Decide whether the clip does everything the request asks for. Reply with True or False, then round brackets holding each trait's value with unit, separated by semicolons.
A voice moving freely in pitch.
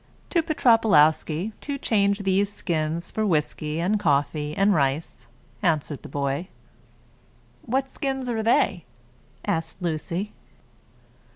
True (5.9 semitones)